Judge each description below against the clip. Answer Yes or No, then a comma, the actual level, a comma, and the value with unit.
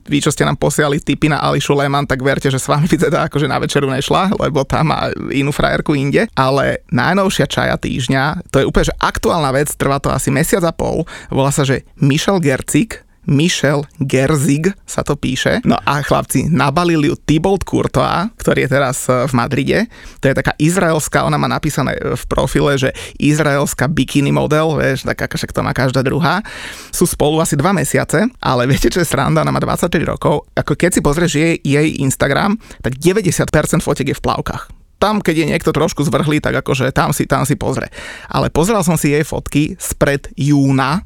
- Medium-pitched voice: Yes, medium, 150 Hz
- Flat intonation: No, average, 3.1 semitones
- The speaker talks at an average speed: No, fast, 190 wpm